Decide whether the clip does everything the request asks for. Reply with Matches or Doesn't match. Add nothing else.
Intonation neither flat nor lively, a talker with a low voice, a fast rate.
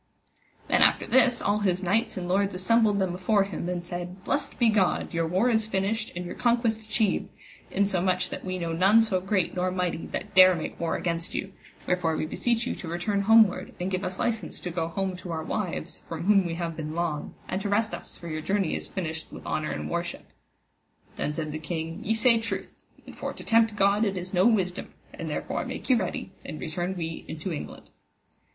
Doesn't match